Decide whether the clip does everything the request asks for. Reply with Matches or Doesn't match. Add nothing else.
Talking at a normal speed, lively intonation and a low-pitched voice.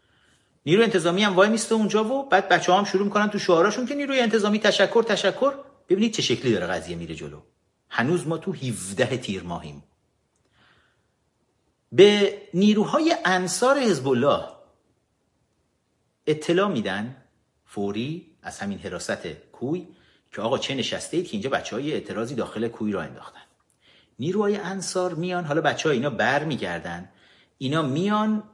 Doesn't match